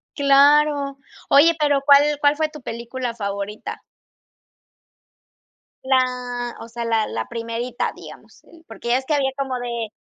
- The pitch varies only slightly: No, average, 3.3 semitones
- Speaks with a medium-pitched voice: No, very high, 255 Hz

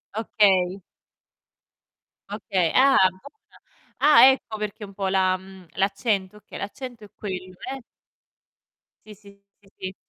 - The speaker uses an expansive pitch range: No, narrow, 2.5 semitones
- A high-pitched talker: Yes, high, 200 Hz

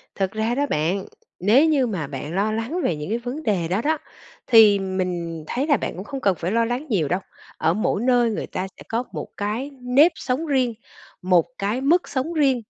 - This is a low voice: No, high, 225 Hz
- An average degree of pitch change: No, wide, 5.8 semitones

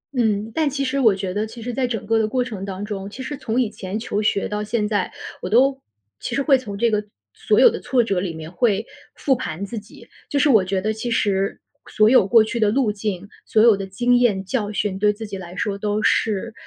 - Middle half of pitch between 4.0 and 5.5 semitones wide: No, average, 3.3 semitones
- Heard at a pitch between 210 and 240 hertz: Yes, high, 215 Hz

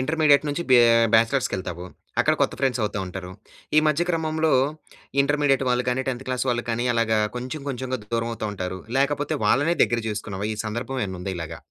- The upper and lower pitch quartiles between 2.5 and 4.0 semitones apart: No, average, 4.8 semitones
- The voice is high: No, low, 125 Hz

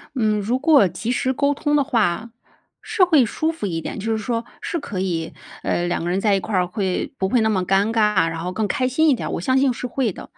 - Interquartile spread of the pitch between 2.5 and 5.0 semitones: No, wide, 5.5 semitones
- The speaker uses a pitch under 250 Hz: Yes, high, 220 Hz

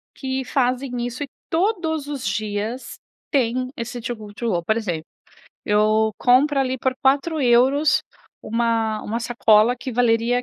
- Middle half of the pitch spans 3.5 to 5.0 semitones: No, average, 3.1 semitones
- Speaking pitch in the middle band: No, high, 245 Hz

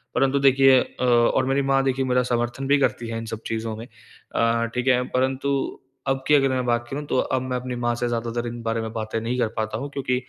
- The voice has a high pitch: No, low, 125 Hz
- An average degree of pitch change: No, narrow, 2.3 semitones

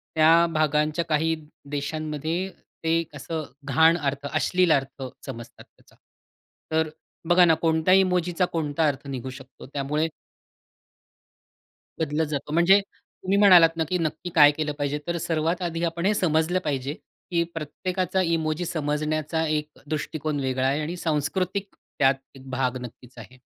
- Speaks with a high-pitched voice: No, medium, 155 Hz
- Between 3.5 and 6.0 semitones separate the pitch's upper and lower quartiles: No, average, 2.8 semitones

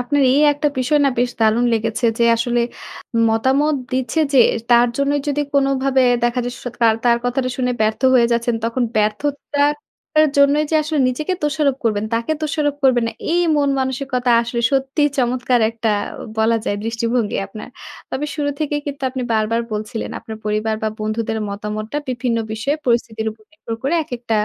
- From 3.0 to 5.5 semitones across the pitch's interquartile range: Yes, average, 3.7 semitones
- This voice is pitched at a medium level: No, high, 245 Hz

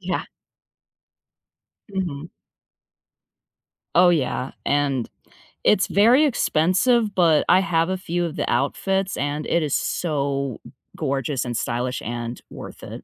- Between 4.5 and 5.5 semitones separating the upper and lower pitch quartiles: Yes, average, 5.2 semitones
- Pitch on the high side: No, medium, 155 Hz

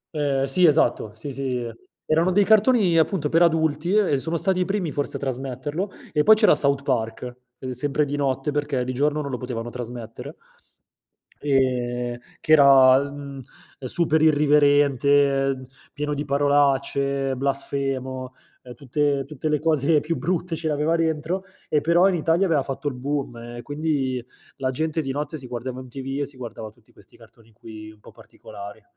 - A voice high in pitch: No, medium, 140 Hz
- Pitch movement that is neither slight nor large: Yes, average, 3.1 semitones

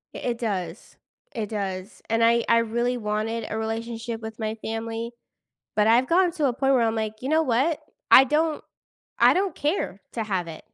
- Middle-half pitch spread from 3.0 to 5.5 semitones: No, narrow, 2.6 semitones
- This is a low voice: No, high, 230 Hz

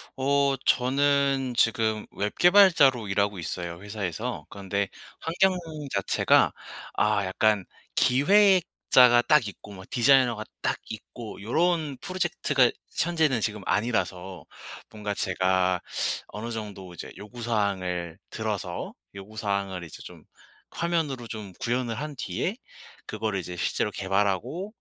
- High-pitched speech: No, low, 110 Hz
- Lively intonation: Yes, wide, 5.7 semitones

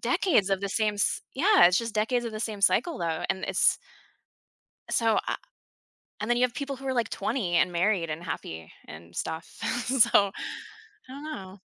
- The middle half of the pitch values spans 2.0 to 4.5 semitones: No, wide, 5.4 semitones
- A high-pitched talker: Yes, high, 215 Hz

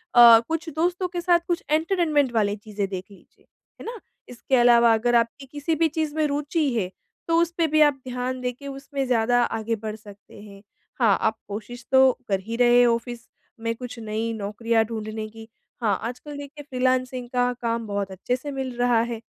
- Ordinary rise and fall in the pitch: Yes, average, 4.2 semitones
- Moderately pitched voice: No, high, 245 Hz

